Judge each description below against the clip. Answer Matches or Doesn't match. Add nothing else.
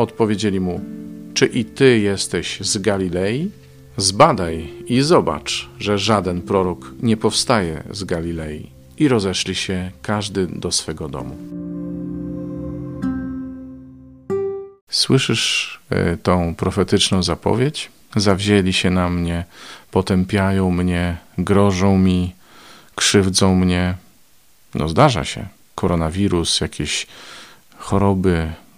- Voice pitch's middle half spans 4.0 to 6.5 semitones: Doesn't match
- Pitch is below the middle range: Matches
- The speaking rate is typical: Doesn't match